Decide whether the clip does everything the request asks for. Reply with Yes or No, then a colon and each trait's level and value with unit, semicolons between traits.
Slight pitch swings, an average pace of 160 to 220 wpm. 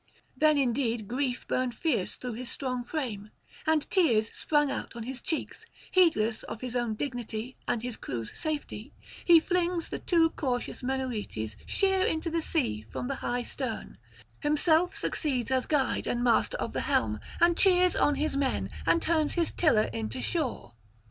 No: average, 5.1 semitones; average, 170 wpm